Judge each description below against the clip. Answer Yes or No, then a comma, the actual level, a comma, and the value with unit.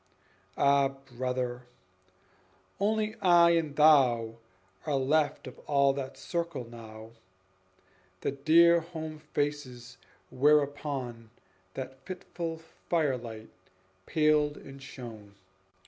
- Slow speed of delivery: Yes, slow, 90 wpm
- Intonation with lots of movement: No, average, 3.9 semitones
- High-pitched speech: No, medium, 140 Hz